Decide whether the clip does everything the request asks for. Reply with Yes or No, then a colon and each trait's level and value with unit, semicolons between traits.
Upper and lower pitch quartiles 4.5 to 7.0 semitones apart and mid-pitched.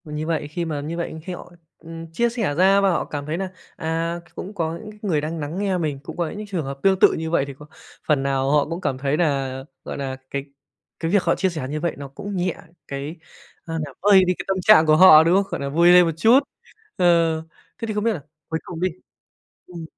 No: average, 3.8 semitones; medium, 165 Hz